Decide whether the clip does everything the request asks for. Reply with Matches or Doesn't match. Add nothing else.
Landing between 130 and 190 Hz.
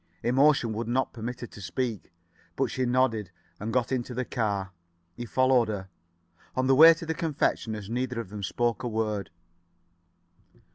Doesn't match